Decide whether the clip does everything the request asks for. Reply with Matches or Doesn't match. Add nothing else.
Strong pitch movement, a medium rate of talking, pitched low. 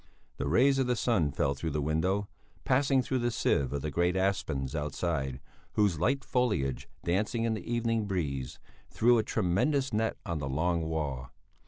Matches